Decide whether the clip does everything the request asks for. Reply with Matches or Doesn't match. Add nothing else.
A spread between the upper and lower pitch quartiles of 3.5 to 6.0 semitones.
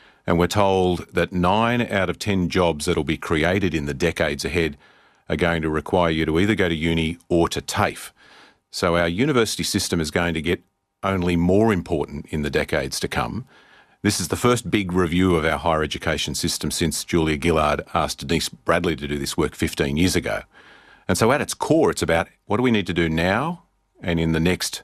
Doesn't match